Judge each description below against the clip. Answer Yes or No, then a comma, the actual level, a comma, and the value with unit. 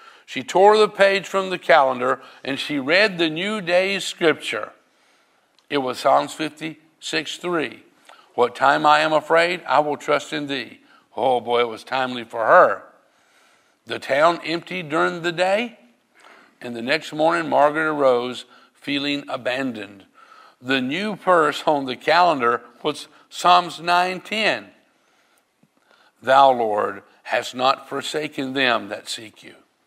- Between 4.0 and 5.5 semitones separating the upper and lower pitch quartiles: Yes, average, 4.4 semitones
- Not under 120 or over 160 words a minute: Yes, average, 140 wpm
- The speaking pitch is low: No, medium, 155 Hz